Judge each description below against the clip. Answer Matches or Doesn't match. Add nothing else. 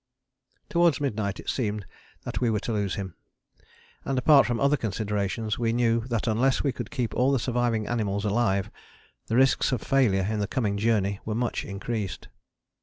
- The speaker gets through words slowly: Doesn't match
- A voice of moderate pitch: Doesn't match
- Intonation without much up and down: Doesn't match